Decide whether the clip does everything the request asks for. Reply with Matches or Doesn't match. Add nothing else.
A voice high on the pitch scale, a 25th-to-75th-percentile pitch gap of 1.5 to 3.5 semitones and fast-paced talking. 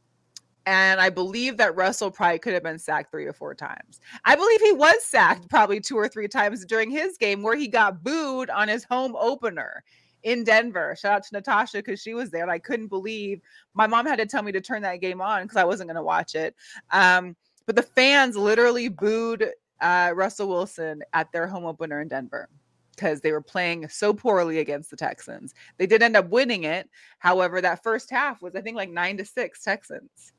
Doesn't match